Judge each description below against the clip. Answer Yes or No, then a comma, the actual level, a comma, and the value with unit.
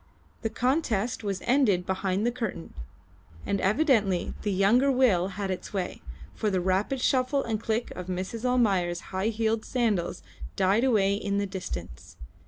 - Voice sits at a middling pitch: No, high, 205 Hz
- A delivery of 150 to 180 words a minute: Yes, average, 155 wpm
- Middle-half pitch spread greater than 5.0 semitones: No, average, 4.2 semitones